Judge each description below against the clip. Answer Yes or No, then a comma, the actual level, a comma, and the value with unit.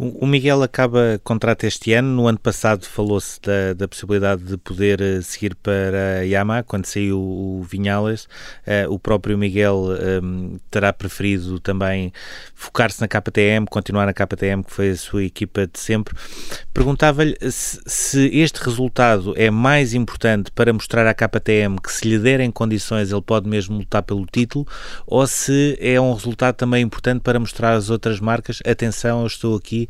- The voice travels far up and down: No, average, 3.1 semitones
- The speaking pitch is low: Yes, low, 110 Hz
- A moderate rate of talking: Yes, average, 170 wpm